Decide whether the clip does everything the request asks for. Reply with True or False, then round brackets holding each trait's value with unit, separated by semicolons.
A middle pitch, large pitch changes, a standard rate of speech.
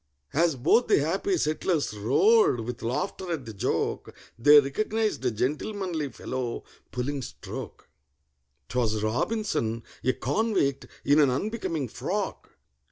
False (145 Hz; 7.5 semitones; 115 wpm)